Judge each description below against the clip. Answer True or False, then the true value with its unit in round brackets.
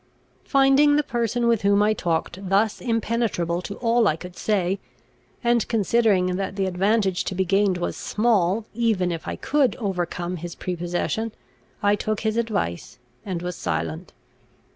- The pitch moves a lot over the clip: False (4.2 semitones)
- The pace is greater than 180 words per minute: False (155 wpm)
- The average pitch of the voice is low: False (200 Hz)